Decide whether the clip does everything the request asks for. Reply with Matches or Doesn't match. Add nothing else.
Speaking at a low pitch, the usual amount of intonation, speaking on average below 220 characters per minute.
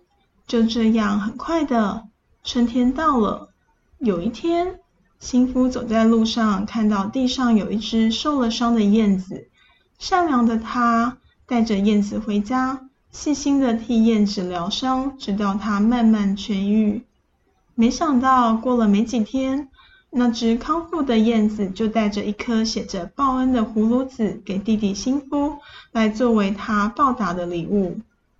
Doesn't match